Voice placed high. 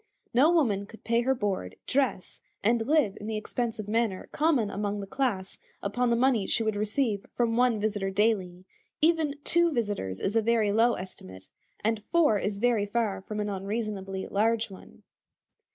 Yes: high, 215 Hz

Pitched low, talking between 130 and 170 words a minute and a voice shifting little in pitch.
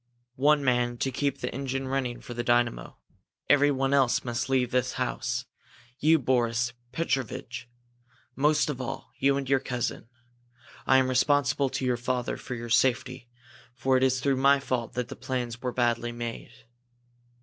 Yes: low, 130 Hz; average, 160 wpm; narrow, 2.0 semitones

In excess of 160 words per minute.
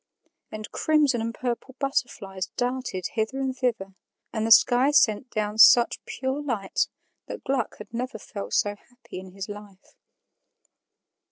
No: average, 145 wpm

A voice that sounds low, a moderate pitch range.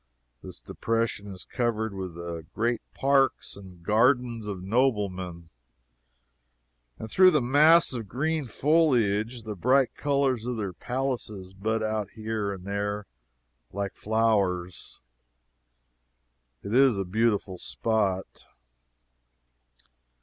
Yes: low, 110 Hz; average, 4.2 semitones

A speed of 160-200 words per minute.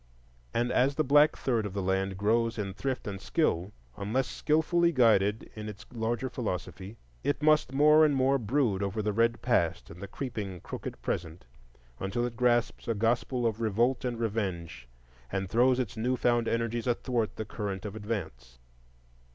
Yes: average, 170 wpm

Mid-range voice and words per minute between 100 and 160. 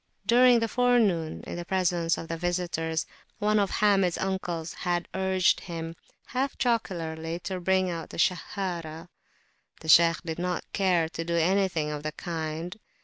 Yes: medium, 175 Hz; average, 155 wpm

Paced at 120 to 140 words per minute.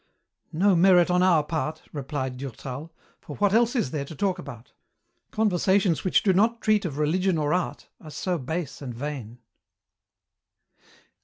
No: average, 155 wpm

